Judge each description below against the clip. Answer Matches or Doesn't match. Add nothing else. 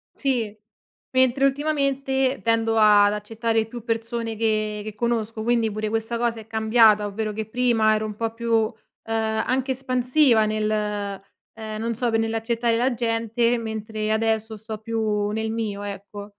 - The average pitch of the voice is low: Doesn't match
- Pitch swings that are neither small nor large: Doesn't match